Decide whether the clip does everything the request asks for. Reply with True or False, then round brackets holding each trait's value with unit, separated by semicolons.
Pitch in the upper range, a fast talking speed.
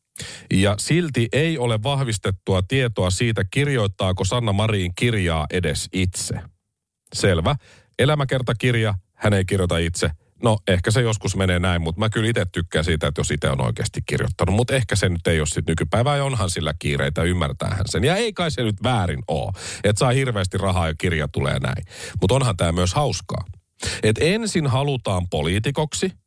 False (100 Hz; 175 wpm)